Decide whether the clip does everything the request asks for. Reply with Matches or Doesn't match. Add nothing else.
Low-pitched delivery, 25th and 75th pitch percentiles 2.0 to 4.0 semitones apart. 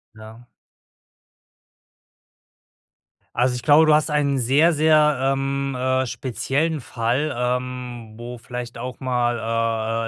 Matches